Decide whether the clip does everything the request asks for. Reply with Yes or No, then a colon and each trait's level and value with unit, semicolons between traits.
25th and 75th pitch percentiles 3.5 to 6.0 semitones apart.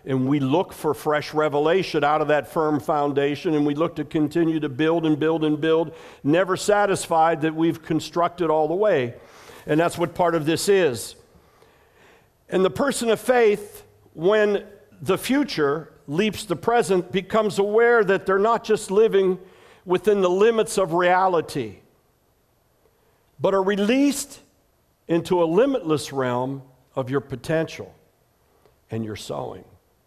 Yes: average, 4.7 semitones